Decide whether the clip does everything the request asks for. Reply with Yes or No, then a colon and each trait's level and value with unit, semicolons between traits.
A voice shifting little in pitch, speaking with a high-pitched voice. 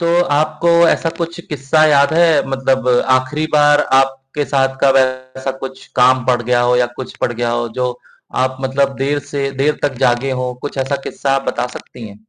No: narrow, 2.1 semitones; low, 135 Hz